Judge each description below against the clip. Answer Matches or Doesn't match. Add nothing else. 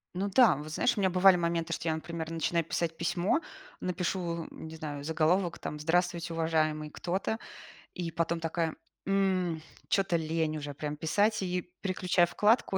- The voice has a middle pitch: Matches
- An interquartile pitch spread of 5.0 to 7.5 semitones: Doesn't match